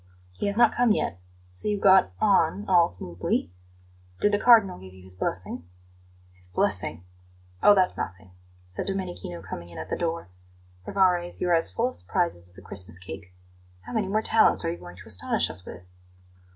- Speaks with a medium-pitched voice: Yes, medium, 165 Hz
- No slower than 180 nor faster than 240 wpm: Yes, average, 185 wpm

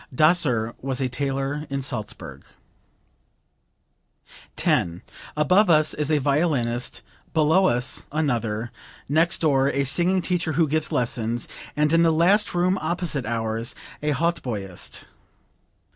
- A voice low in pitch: No, medium, 145 Hz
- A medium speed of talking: No, slow, 120 wpm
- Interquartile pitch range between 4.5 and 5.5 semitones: Yes, average, 5.1 semitones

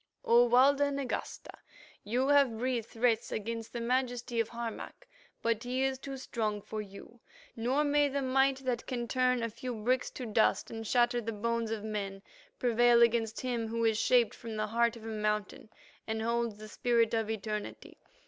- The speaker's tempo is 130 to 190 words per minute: Yes, average, 180 wpm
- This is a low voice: No, high, 235 Hz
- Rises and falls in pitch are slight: Yes, narrow, 2.2 semitones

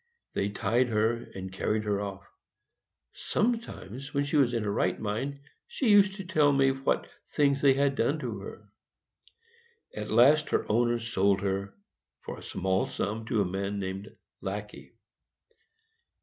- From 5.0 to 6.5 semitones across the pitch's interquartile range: Yes, wide, 5.6 semitones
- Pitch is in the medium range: No, low, 115 Hz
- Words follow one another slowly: No, average, 155 wpm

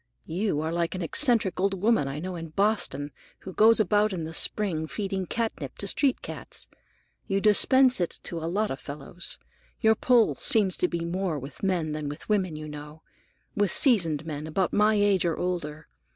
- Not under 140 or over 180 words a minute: No, average, 190 wpm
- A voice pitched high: No, medium, 180 Hz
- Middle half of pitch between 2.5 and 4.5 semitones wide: No, average, 4.9 semitones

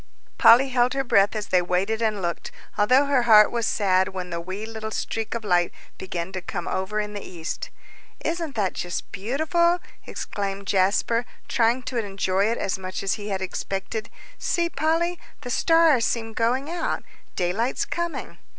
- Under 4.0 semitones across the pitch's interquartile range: No, average, 4.8 semitones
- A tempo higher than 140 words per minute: Yes, average, 170 wpm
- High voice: Yes, high, 215 Hz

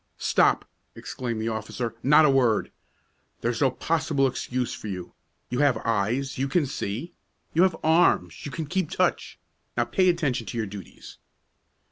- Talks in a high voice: No, low, 130 Hz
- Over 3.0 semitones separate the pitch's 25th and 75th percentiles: Yes, average, 5.3 semitones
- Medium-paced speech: Yes, average, 160 wpm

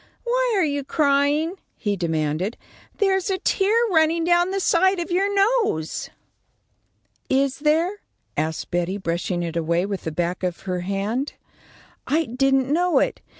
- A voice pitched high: Yes, very high, 280 Hz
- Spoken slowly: No, average, 150 wpm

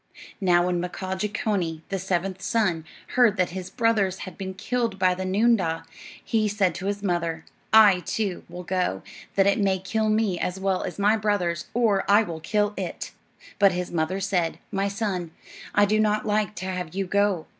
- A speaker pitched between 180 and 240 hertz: Yes, high, 190 Hz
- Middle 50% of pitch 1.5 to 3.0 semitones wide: Yes, narrow, 2.6 semitones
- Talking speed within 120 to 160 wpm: No, average, 190 wpm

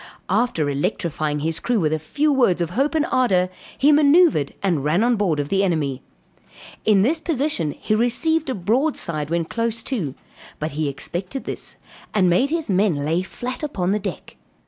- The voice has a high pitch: Yes, high, 195 Hz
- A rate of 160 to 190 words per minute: Yes, average, 180 wpm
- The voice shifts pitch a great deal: Yes, wide, 8.3 semitones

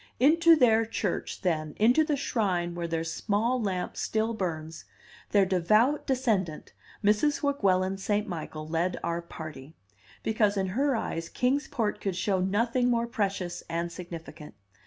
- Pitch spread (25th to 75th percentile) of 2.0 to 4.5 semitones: No, average, 5.2 semitones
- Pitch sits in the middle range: No, high, 200 Hz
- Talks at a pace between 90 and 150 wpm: Yes, average, 145 wpm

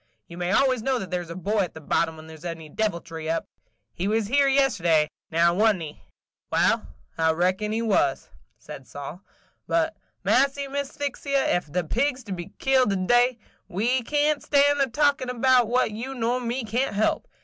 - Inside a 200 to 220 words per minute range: Yes, fast, 205 wpm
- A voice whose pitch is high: Yes, high, 220 Hz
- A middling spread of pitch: No, wide, 7.4 semitones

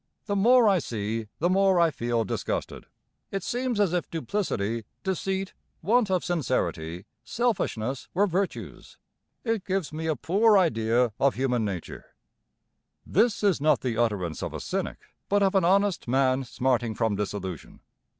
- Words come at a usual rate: Yes, average, 150 wpm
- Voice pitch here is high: No, medium, 160 Hz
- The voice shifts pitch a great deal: Yes, wide, 9.0 semitones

